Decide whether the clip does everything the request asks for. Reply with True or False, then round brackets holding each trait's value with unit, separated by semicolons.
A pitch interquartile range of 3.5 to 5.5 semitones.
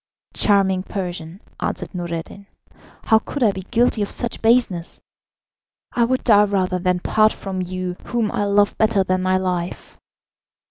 False (2.9 semitones)